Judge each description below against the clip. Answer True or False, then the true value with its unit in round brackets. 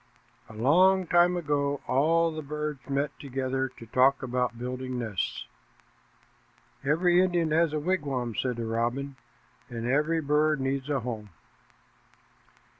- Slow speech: True (130 wpm)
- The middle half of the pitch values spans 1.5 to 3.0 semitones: False (3.7 semitones)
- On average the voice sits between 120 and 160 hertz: True (140 Hz)